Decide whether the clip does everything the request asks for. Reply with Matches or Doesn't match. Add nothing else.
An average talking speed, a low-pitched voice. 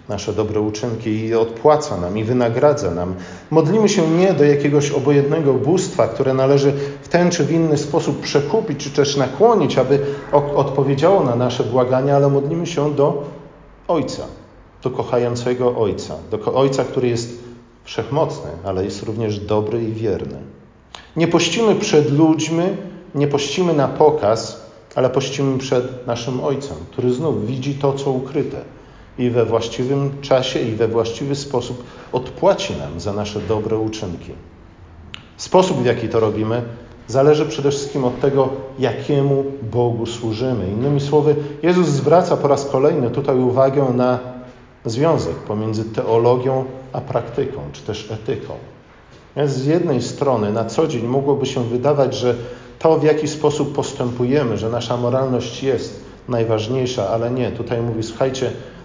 Matches